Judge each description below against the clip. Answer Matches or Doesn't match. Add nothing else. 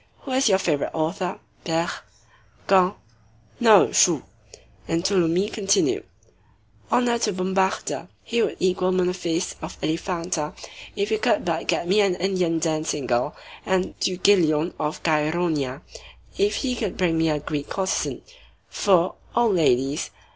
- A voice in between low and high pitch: Matches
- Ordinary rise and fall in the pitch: Matches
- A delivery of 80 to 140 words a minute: Matches